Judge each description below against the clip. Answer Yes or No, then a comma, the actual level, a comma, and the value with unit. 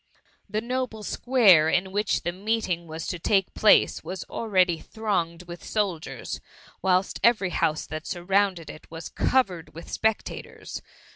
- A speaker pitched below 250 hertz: Yes, high, 190 Hz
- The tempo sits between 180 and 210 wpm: No, average, 145 wpm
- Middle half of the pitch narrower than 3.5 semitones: No, average, 4.0 semitones